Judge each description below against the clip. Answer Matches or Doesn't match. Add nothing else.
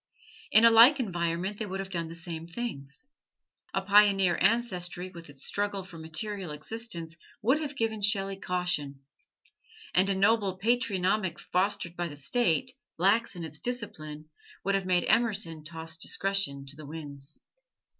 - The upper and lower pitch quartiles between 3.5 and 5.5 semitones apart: Matches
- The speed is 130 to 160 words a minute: Matches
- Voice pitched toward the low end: Doesn't match